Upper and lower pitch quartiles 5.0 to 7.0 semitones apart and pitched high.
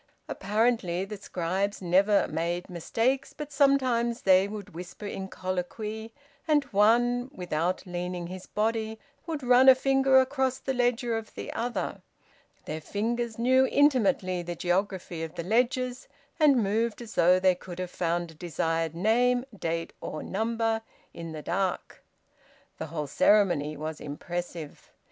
Yes: wide, 5.6 semitones; high, 205 Hz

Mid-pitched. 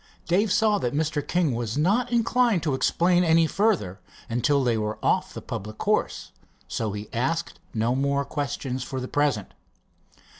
Yes: medium, 145 Hz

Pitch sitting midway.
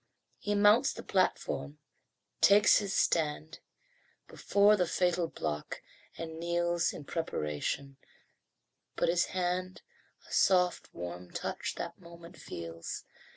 Yes: medium, 170 Hz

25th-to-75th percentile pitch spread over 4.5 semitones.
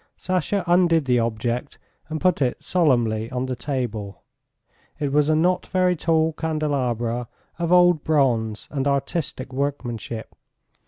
Yes: average, 5.0 semitones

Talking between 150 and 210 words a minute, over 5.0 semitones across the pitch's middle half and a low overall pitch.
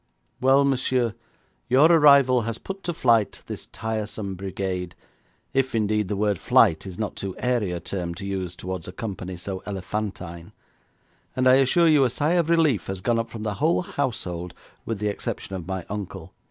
Yes: average, 180 wpm; wide, 5.5 semitones; low, 105 Hz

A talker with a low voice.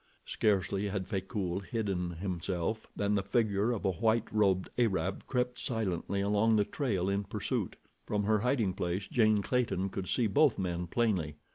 Yes: low, 100 Hz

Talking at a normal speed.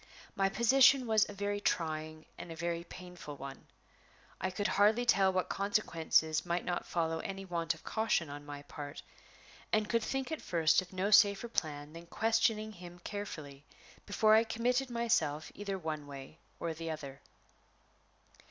Yes: average, 160 wpm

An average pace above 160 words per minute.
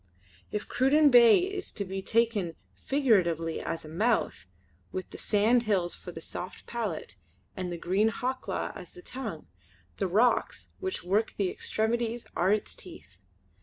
No: average, 150 wpm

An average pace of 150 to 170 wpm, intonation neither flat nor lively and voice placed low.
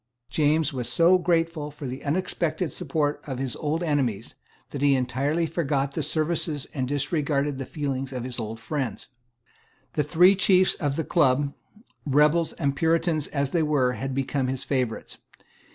No: average, 160 wpm; average, 3.3 semitones; medium, 145 Hz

